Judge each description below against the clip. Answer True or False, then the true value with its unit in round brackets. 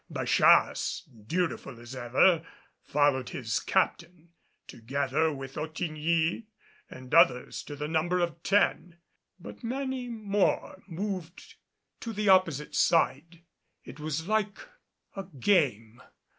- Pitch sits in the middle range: True (165 Hz)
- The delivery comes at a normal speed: False (110 wpm)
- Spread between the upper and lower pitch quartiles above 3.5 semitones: True (5.2 semitones)